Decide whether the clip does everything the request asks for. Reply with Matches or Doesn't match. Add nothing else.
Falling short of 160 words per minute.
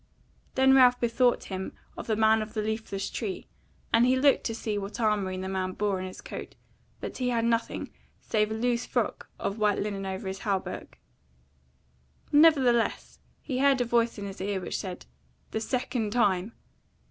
Doesn't match